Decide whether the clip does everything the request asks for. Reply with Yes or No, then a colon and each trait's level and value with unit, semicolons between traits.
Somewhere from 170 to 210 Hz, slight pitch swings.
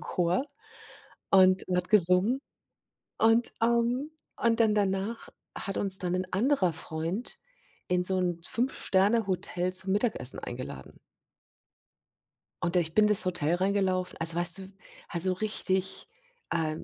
No: medium, 185 Hz; average, 3.1 semitones